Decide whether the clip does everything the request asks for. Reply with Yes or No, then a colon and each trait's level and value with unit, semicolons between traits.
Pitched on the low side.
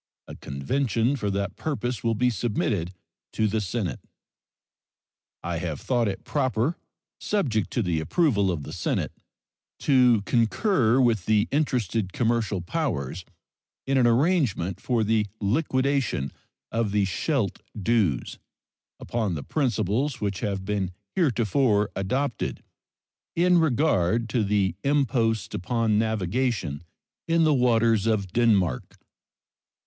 Yes: low, 110 Hz